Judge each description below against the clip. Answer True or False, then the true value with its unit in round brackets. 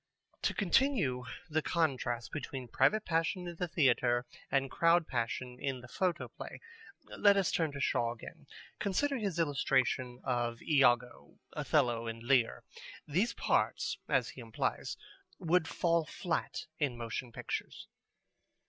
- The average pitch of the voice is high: False (140 Hz)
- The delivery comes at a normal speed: False (130 wpm)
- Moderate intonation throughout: False (5.9 semitones)